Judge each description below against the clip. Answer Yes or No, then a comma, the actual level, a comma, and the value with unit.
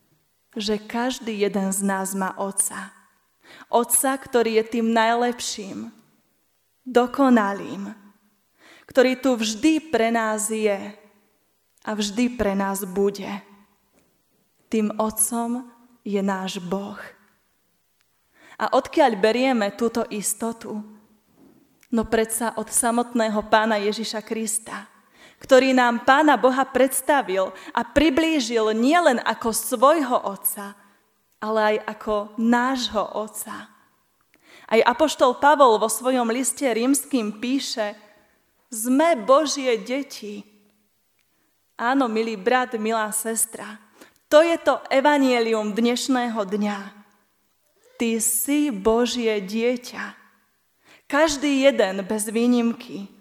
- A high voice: Yes, high, 225 Hz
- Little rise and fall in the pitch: No, average, 3.2 semitones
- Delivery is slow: Yes, slow, 100 wpm